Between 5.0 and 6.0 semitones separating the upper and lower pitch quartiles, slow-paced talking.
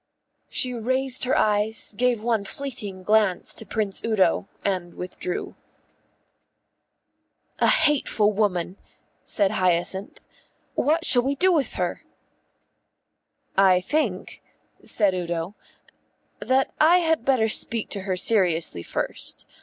Yes: wide, 5.4 semitones; slow, 115 wpm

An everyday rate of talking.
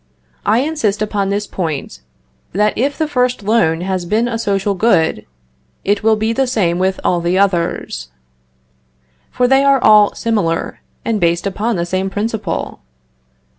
Yes: average, 155 wpm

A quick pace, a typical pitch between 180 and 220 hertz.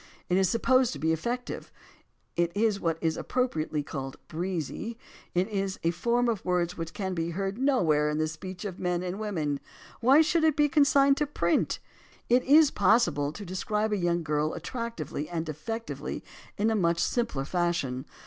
No: average, 175 wpm; medium, 185 Hz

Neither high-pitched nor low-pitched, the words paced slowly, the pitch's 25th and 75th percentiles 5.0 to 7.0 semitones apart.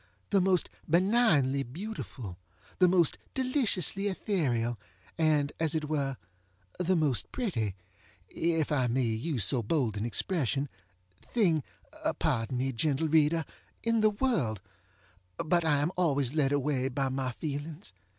Yes: medium, 150 Hz; slow, 130 wpm; wide, 5.4 semitones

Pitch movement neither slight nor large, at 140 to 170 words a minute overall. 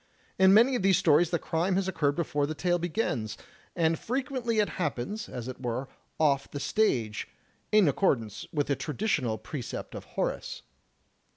No: wide, 6.2 semitones; average, 165 wpm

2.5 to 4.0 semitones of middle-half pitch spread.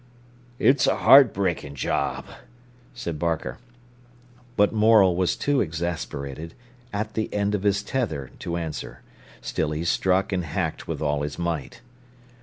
No: average, 4.7 semitones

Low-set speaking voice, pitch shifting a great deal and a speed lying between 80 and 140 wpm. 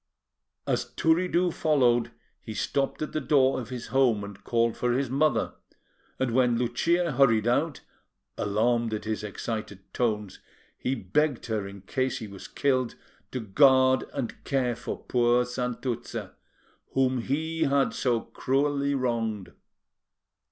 No: low, 125 Hz; average, 3.3 semitones; slow, 135 wpm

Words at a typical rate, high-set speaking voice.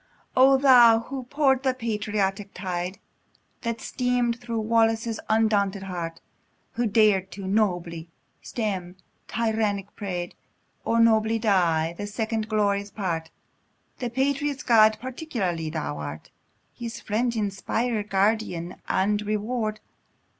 No: slow, 115 wpm; high, 215 Hz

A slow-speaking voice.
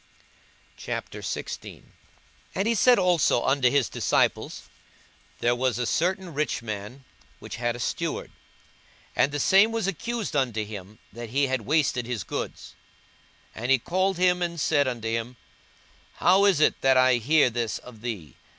No: average, 160 wpm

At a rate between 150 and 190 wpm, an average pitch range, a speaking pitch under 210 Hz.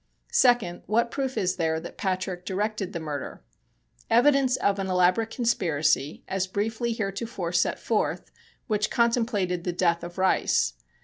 No: average, 140 wpm; average, 4.4 semitones; high, 190 Hz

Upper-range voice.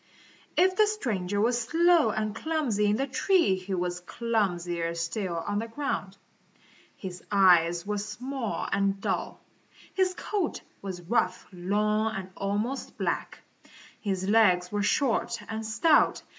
Yes: high, 210 Hz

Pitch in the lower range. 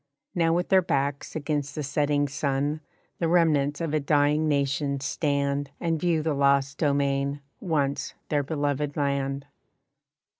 No: medium, 145 Hz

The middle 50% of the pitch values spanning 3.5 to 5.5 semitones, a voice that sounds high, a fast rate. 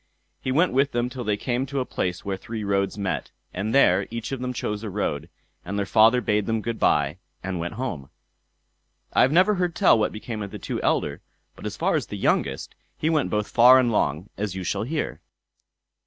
No: average, 4.6 semitones; low, 110 Hz; fast, 220 wpm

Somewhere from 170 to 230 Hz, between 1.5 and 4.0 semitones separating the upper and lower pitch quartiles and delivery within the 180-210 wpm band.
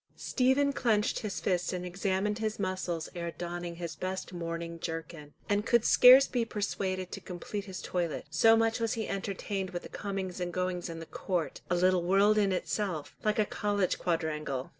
Yes: medium, 185 Hz; average, 3.2 semitones; average, 185 wpm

